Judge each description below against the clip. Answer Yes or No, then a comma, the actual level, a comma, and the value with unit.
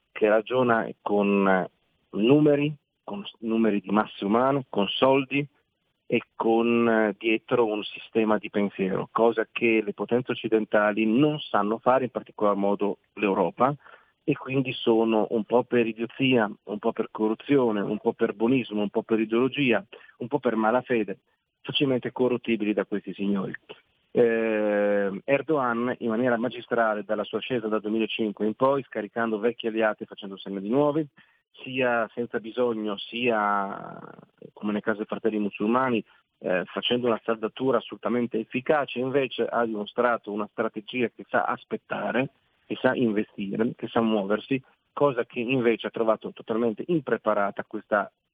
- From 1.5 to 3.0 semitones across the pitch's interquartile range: Yes, average, 2.7 semitones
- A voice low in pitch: Yes, low, 115 Hz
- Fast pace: No, average, 145 wpm